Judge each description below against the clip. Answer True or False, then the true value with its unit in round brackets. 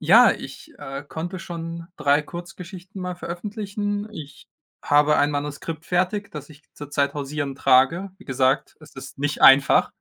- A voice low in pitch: False (155 Hz)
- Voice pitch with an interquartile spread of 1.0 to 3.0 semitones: False (4.0 semitones)